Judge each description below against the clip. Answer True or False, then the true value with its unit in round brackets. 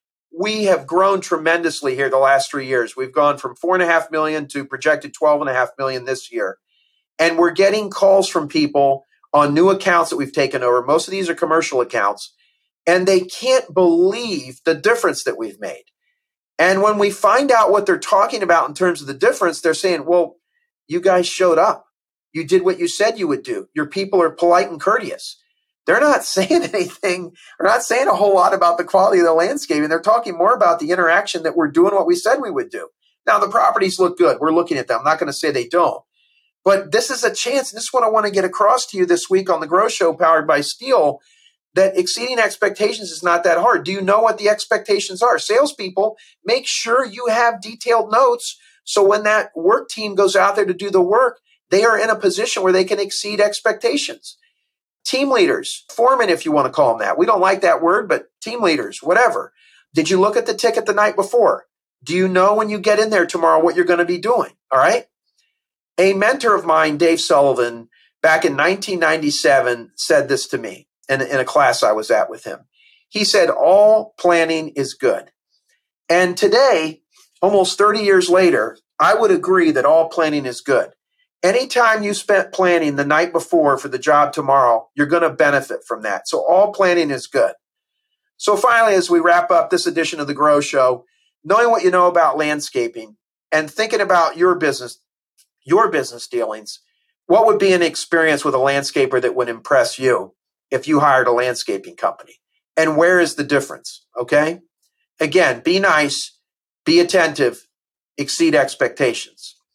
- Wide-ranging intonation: True (6.3 semitones)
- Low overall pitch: False (185 Hz)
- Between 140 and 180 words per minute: False (200 wpm)